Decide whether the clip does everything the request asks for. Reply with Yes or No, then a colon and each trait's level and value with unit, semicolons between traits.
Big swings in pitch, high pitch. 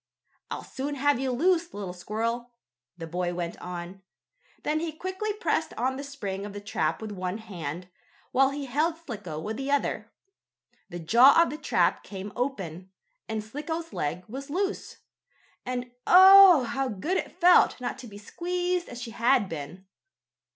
Yes: wide, 7.8 semitones; high, 245 Hz